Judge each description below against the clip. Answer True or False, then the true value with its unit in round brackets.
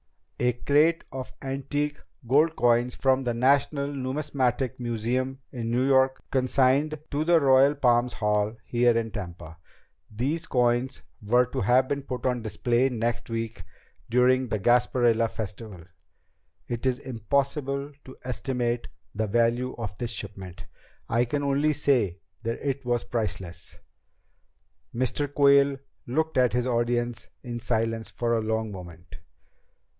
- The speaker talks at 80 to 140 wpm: True (135 wpm)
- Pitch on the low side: True (125 Hz)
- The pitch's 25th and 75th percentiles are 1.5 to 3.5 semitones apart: True (2.8 semitones)